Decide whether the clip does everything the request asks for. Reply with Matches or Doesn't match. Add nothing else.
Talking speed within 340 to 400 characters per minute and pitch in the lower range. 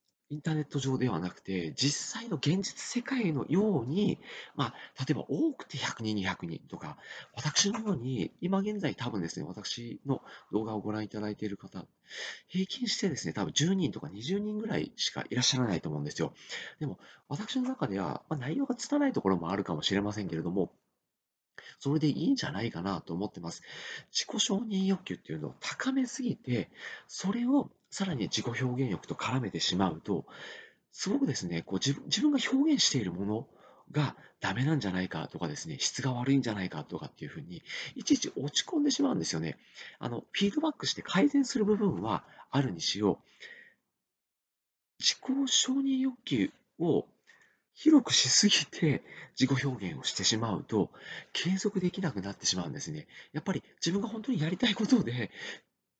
Doesn't match